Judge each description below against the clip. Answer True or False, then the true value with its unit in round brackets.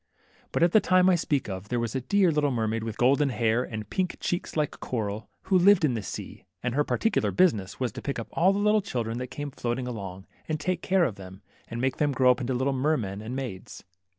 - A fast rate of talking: True (240 wpm)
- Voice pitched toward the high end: False (130 Hz)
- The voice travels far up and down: True (6.0 semitones)